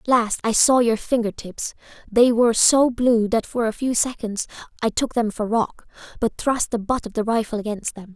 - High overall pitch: Yes, high, 225 Hz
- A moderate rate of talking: No, fast, 220 wpm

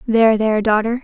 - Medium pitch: No, high, 220 Hz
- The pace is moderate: Yes, average, 175 wpm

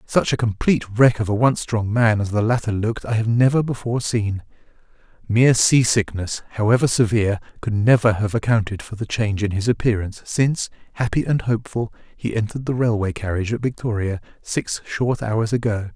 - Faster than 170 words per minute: Yes, average, 180 wpm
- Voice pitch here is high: No, low, 110 Hz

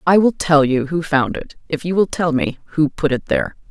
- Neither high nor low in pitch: Yes, medium, 160 Hz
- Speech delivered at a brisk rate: Yes, fast, 260 wpm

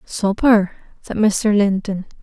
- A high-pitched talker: Yes, high, 205 Hz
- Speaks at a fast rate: No, slow, 110 wpm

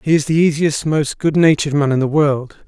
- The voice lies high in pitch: No, medium, 150 Hz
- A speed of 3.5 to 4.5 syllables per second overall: No, 5.5 syllables/s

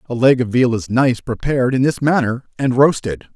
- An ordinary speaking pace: No, fast, 215 wpm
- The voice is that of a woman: No, male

